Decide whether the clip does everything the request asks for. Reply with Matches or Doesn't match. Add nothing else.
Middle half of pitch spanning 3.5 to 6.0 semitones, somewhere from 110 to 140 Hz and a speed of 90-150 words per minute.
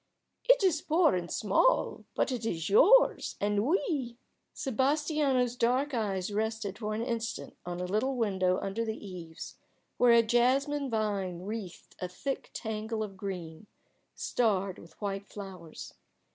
Doesn't match